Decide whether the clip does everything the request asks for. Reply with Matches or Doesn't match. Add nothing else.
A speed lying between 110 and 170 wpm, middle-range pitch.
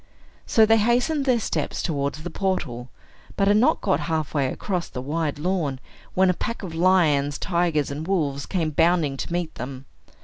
Doesn't match